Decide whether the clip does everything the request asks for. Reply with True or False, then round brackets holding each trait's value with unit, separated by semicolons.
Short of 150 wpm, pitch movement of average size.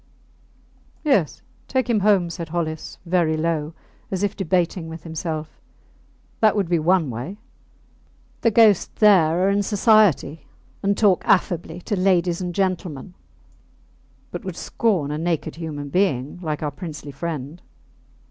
True (140 wpm; 3.8 semitones)